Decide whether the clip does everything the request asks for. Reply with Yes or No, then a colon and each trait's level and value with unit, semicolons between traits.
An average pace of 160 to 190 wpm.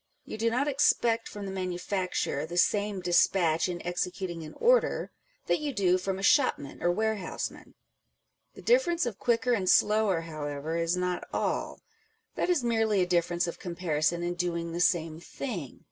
Yes: average, 170 wpm